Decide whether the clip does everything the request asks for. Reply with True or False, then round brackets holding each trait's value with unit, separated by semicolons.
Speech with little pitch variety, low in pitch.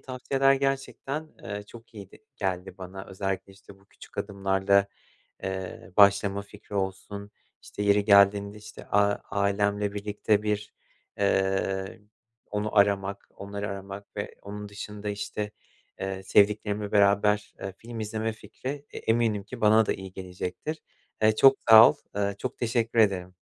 True (1.6 semitones; 100 Hz)